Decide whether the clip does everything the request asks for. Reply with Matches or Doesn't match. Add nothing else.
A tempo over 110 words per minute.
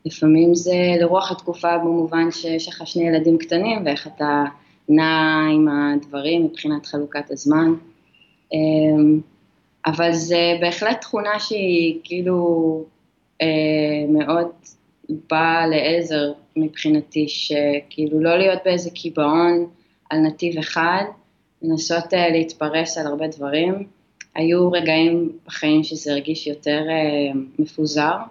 Doesn't match